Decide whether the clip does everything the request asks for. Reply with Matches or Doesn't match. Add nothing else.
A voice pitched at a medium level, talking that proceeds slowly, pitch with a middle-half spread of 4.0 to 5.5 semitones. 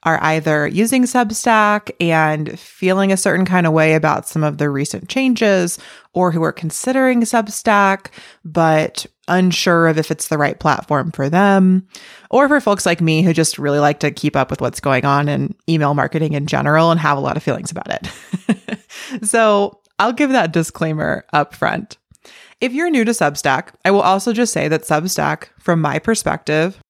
Doesn't match